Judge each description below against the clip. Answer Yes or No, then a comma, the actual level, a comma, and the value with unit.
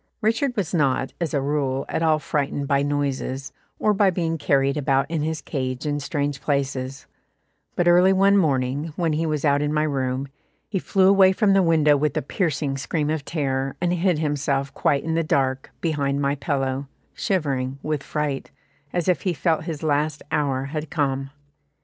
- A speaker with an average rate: Yes, average, 185 wpm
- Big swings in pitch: No, average, 3.1 semitones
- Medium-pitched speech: Yes, medium, 150 Hz